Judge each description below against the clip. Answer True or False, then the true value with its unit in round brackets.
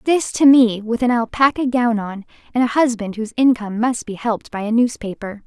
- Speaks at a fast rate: True (210 wpm)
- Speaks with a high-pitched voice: True (235 Hz)